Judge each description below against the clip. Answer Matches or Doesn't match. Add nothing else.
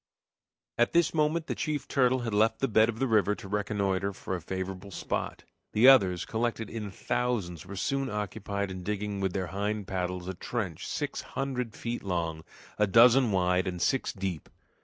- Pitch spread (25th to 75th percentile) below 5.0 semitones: Matches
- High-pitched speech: Doesn't match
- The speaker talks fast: Doesn't match